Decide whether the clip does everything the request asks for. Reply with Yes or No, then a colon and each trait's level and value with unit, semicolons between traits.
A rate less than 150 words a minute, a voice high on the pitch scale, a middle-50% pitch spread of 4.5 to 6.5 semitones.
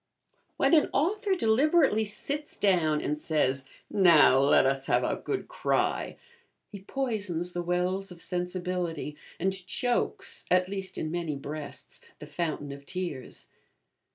No: slow, 135 wpm; medium, 180 Hz; average, 5.2 semitones